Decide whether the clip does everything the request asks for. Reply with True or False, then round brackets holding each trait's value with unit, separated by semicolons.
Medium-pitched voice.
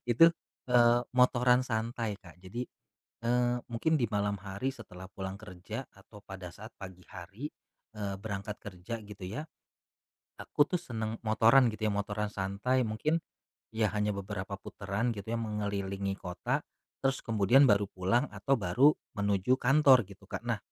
False (105 Hz)